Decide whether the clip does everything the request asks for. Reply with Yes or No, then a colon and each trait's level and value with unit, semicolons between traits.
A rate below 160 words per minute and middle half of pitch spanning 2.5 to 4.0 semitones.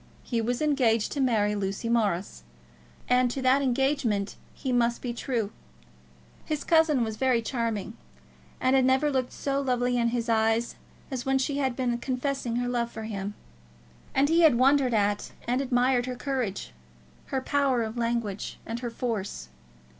No: average, 165 wpm; average, 2.8 semitones